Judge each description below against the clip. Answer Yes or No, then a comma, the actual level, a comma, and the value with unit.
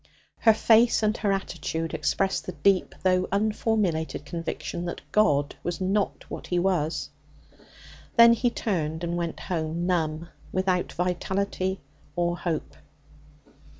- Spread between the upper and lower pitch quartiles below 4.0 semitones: Yes, average, 3.0 semitones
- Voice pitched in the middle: Yes, medium, 180 Hz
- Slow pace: Yes, slow, 125 wpm